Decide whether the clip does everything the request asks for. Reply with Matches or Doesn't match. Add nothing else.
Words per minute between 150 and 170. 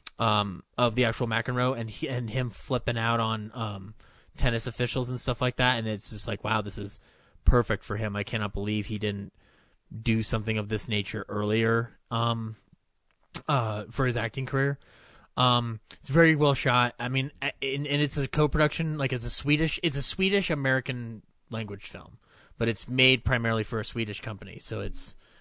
Doesn't match